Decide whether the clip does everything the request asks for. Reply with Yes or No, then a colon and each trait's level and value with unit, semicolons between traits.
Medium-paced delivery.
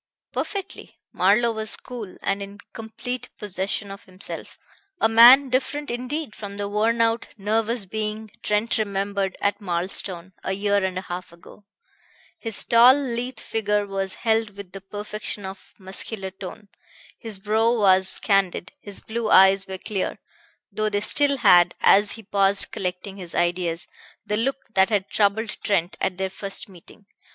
Yes: average, 155 wpm